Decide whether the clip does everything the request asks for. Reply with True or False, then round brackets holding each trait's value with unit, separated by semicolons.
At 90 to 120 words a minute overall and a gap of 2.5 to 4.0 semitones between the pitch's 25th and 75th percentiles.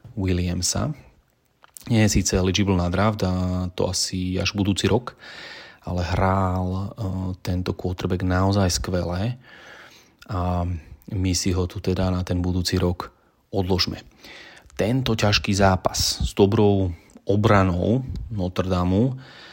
False (115 wpm; 2.0 semitones)